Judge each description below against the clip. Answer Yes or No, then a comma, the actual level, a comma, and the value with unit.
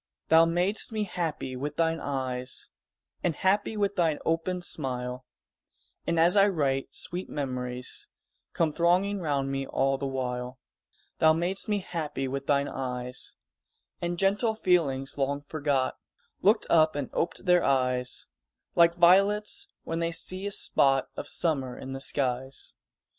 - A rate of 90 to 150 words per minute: Yes, average, 145 wpm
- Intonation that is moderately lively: Yes, average, 4.9 semitones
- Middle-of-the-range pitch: Yes, medium, 155 Hz